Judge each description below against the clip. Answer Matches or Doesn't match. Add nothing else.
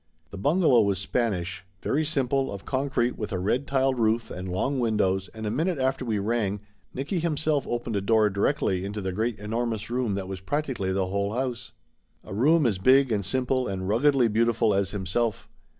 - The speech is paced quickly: Doesn't match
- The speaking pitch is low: Matches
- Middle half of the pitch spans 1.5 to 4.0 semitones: Doesn't match